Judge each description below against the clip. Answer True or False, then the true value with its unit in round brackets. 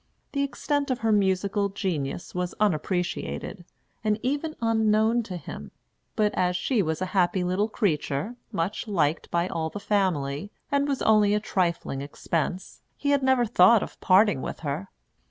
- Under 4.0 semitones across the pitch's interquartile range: False (4.3 semitones)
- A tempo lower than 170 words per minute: True (160 wpm)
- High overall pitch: True (200 Hz)